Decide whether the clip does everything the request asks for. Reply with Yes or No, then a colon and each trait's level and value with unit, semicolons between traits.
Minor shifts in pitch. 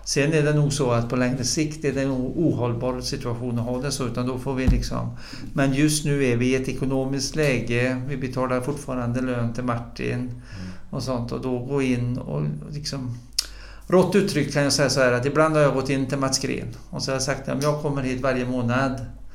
Yes: narrow, 2.3 semitones